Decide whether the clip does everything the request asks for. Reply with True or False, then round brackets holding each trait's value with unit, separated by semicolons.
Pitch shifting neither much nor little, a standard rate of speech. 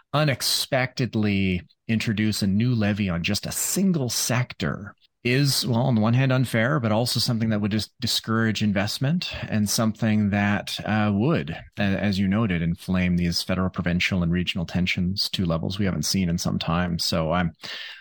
True (4.1 semitones; 170 wpm)